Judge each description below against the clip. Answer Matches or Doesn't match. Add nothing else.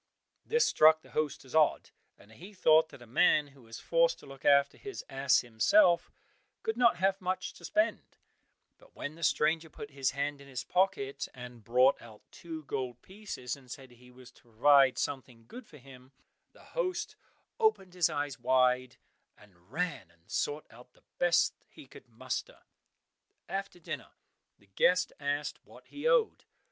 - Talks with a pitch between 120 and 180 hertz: Matches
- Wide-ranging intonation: Matches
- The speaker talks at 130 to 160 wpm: Doesn't match